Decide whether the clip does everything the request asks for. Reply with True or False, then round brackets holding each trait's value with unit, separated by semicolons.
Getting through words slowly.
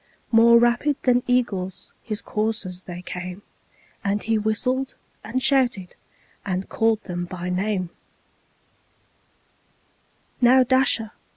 True (105 wpm)